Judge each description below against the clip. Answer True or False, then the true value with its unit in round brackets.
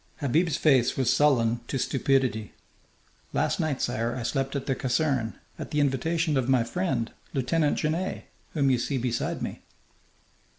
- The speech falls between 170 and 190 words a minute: False (155 wpm)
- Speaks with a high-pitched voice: False (135 Hz)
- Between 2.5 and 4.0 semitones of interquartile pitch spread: True (3.7 semitones)